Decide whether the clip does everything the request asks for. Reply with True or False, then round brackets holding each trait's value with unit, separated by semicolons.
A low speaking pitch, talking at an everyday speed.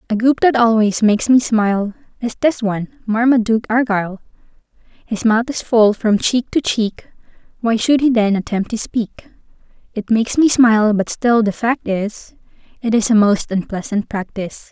False (225 Hz; 170 wpm)